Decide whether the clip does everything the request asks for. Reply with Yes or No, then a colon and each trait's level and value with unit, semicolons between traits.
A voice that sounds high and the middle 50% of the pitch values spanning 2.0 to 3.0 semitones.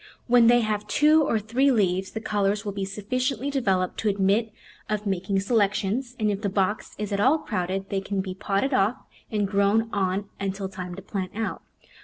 Yes: high, 205 Hz; narrow, 2.6 semitones